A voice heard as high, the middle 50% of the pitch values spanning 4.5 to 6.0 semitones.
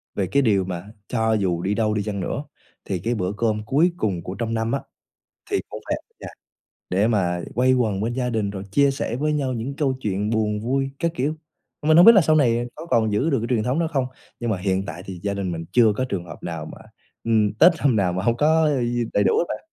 No: low, 110 Hz; average, 5.0 semitones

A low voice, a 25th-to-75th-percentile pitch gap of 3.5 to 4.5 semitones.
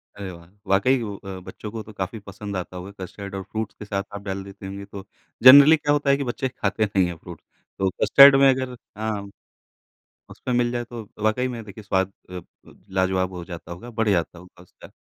Yes: low, 100 Hz; average, 4.1 semitones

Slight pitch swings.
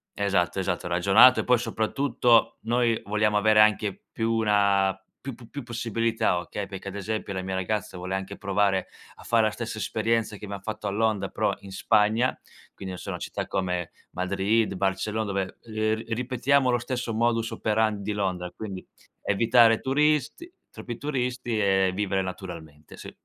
No: average, 3.0 semitones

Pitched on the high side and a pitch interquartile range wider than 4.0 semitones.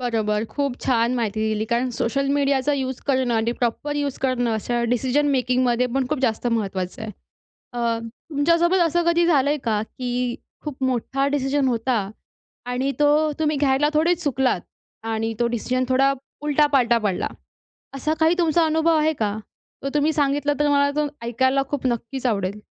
No: very high, 260 Hz; average, 3.6 semitones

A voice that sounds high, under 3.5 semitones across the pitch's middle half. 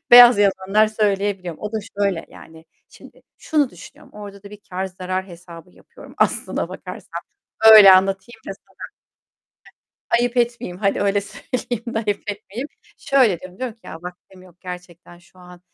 Yes: high, 195 Hz; average, 3.1 semitones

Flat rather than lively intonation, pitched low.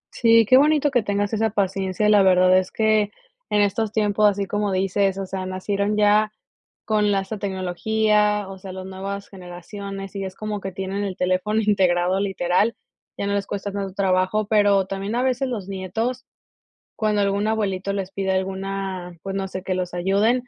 No: narrow, 1.9 semitones; high, 200 Hz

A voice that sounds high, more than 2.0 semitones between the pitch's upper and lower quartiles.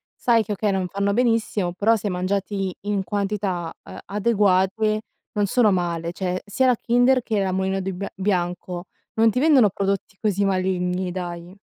Yes: high, 195 Hz; narrow, 2.5 semitones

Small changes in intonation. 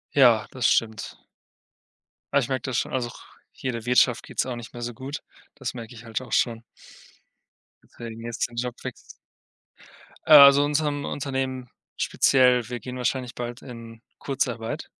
Yes: narrow, 2.1 semitones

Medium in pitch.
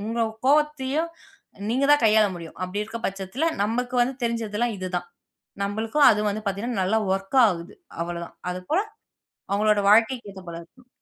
No: high, 215 Hz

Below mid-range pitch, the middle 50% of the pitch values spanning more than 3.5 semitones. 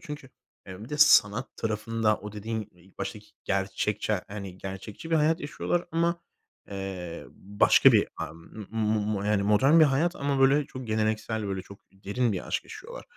Yes: low, 110 Hz; average, 5.3 semitones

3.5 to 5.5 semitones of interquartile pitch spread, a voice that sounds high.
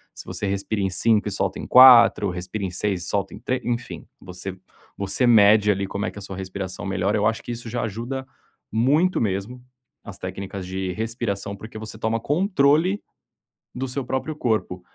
No: average, 3.9 semitones; low, 105 Hz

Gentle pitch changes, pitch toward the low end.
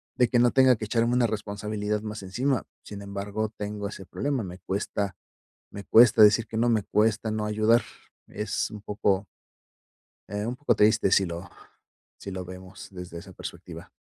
Yes: narrow, 2.3 semitones; low, 105 Hz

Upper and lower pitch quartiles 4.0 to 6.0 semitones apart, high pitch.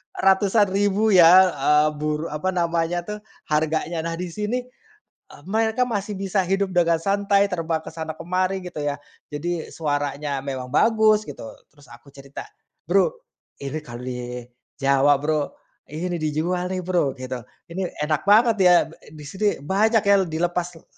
No: average, 4.5 semitones; medium, 170 Hz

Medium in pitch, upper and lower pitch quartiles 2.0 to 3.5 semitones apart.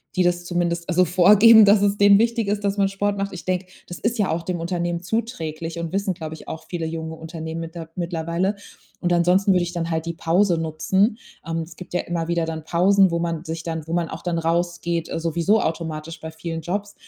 Yes: medium, 175 Hz; average, 2.9 semitones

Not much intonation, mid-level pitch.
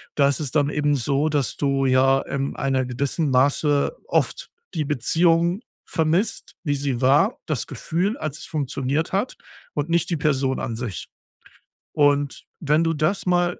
No: average, 3.1 semitones; medium, 145 Hz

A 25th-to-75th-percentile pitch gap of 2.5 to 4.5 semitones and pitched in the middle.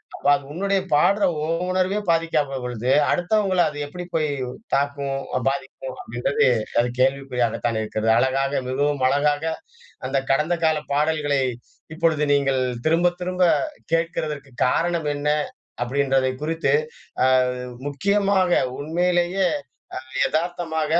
Yes: average, 4.2 semitones; medium, 150 Hz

